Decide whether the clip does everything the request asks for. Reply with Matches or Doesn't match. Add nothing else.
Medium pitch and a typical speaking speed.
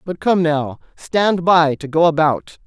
Matches